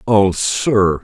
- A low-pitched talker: Yes, low, 100 Hz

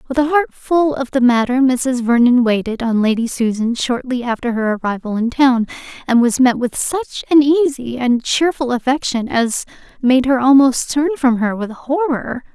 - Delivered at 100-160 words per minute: No, average, 180 wpm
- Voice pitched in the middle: No, very high, 255 Hz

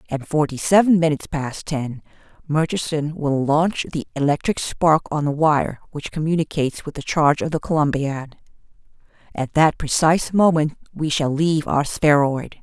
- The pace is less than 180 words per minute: Yes, average, 150 wpm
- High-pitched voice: No, medium, 150 Hz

